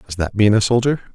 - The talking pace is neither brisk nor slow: No, fast, 265 wpm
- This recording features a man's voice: Yes, male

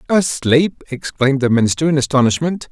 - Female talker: No, male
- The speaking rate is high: No, slow, 130 wpm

